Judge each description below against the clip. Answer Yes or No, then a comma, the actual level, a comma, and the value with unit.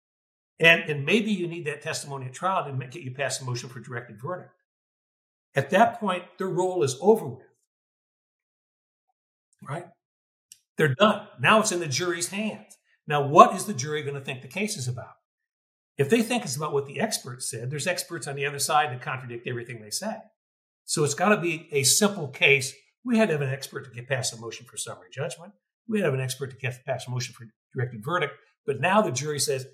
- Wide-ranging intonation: Yes, wide, 5.7 semitones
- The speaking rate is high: Yes, fast, 220 wpm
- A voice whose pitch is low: No, medium, 145 Hz